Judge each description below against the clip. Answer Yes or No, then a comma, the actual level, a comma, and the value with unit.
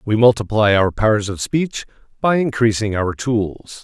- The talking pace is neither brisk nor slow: Yes, average, 155 wpm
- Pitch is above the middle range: No, low, 110 Hz